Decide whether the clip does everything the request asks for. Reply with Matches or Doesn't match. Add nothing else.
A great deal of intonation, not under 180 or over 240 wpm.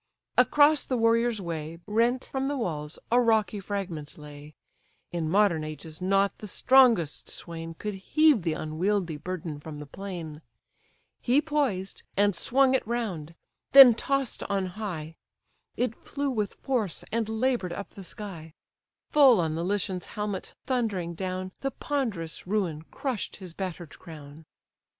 Doesn't match